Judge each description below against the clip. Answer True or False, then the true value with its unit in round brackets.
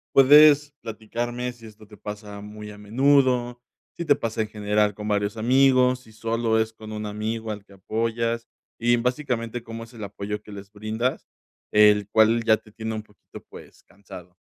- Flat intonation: True (2.3 semitones)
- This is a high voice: False (110 Hz)